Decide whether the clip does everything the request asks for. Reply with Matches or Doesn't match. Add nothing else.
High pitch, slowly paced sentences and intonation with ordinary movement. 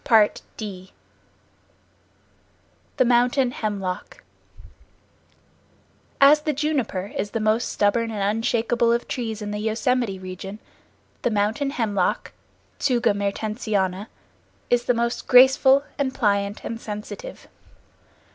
Matches